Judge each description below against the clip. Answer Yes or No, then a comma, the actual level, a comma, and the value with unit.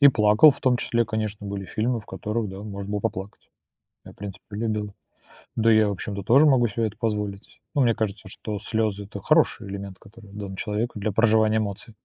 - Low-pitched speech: Yes, low, 105 Hz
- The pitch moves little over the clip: Yes, narrow, 2.1 semitones